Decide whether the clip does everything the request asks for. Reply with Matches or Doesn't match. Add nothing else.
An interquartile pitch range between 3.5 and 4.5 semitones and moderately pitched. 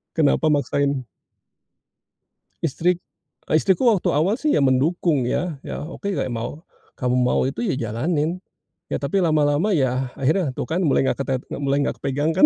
Matches